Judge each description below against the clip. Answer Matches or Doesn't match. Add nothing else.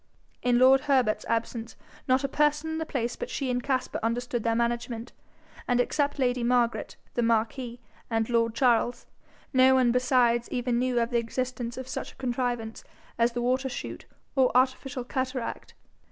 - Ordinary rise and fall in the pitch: Doesn't match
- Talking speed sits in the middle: Matches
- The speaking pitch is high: Matches